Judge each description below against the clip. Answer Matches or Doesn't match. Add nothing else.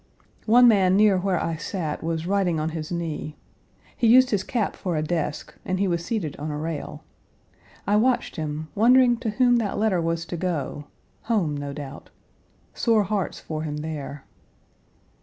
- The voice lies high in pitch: Doesn't match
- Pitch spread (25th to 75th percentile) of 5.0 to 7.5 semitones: Matches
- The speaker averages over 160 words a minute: Matches